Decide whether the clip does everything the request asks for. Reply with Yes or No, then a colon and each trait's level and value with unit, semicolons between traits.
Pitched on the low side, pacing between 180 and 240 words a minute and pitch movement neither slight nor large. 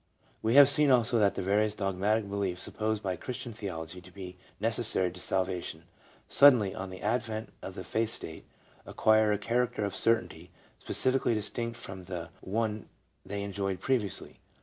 No: low, 105 Hz; average, 155 wpm; average, 3.5 semitones